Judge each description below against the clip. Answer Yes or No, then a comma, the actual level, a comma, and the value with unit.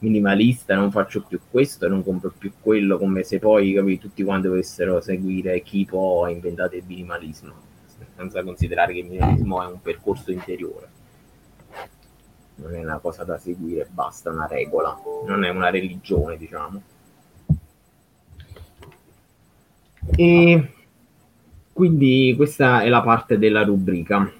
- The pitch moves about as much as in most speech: Yes, average, 4.1 semitones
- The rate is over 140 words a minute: No, average, 130 wpm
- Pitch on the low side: Yes, very low, 95 Hz